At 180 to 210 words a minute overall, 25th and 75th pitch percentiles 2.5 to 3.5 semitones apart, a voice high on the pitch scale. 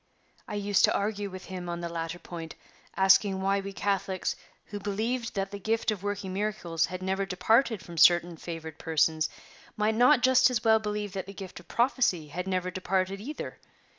Yes: average, 190 wpm; average, 2.9 semitones; high, 195 Hz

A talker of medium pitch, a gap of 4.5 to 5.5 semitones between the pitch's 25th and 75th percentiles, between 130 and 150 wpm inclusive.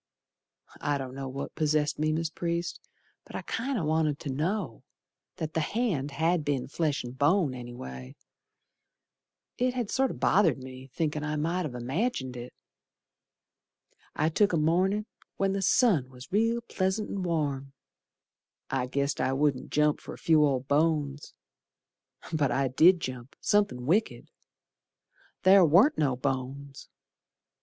Yes: medium, 150 Hz; average, 5.2 semitones; average, 145 wpm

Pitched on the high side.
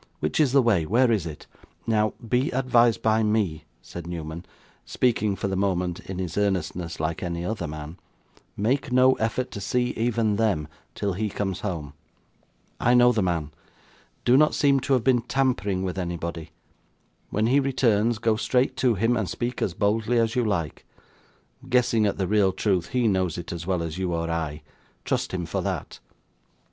No: low, 105 Hz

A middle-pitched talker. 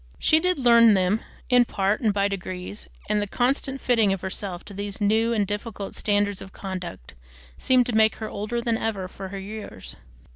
No: high, 205 Hz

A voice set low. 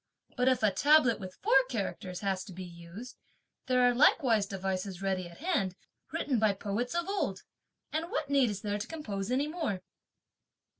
No: high, 215 Hz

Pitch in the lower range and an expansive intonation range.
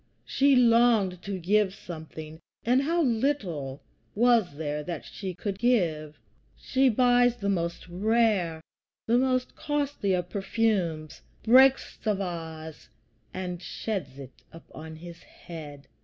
No: high, 190 Hz; wide, 6.6 semitones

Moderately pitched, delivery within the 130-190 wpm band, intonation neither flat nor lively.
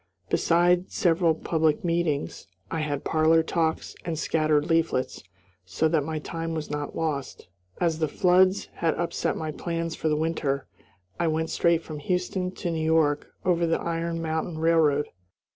No: medium, 160 Hz; average, 160 wpm; narrow, 1.5 semitones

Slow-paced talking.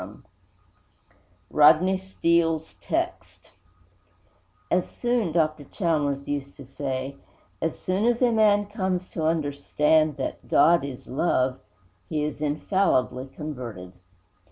Yes: slow, 115 wpm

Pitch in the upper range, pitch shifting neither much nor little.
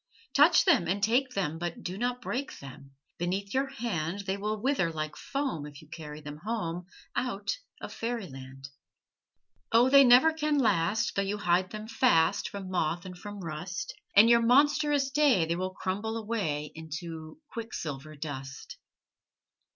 No: high, 195 Hz; wide, 6.8 semitones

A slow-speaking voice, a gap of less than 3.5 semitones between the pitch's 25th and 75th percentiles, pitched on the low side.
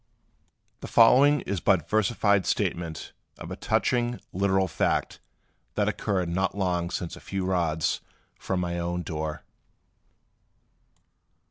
Yes: slow, 120 wpm; average, 2.9 semitones; very low, 95 Hz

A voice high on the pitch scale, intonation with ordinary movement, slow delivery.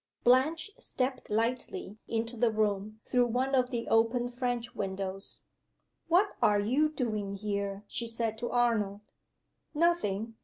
Yes: high, 230 Hz; average, 3.2 semitones; slow, 130 wpm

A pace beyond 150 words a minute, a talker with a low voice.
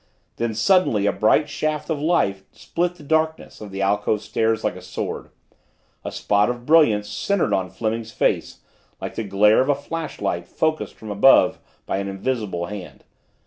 Yes: average, 170 wpm; low, 110 Hz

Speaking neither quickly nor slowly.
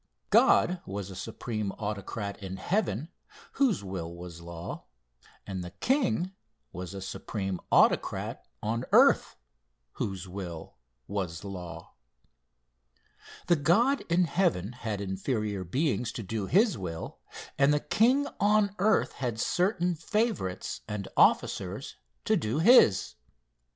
No: slow, 120 wpm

